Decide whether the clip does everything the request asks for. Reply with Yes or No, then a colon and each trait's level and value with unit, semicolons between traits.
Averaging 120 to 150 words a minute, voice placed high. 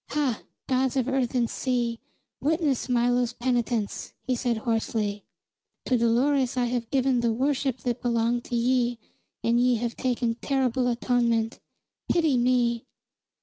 Yes: average, 140 wpm; high, 245 Hz